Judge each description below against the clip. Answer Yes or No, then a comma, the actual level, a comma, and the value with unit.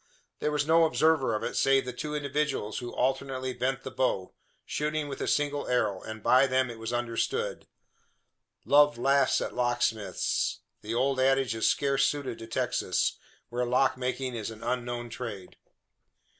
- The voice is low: Yes, low, 130 Hz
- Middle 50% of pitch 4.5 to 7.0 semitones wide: No, average, 2.8 semitones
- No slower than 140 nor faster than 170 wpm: Yes, average, 165 wpm